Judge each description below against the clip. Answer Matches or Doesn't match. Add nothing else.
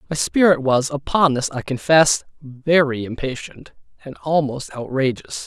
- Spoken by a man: Matches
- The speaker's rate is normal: Doesn't match